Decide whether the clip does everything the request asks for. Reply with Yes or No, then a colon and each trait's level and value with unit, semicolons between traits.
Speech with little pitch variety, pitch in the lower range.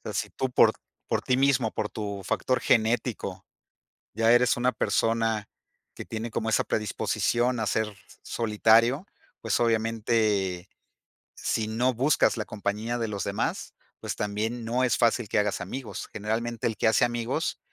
Yes: narrow, 2.1 semitones; low, 115 Hz